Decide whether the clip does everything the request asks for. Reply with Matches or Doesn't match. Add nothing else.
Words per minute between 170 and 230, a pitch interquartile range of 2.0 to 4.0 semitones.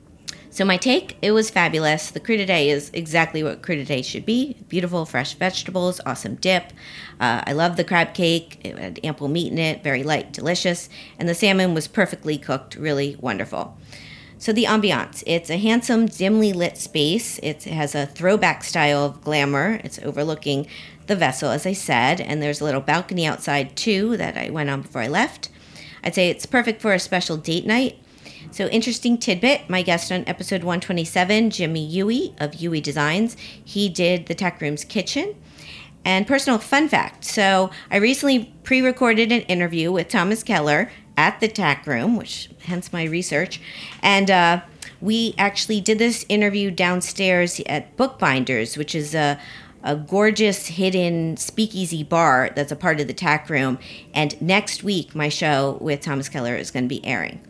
Doesn't match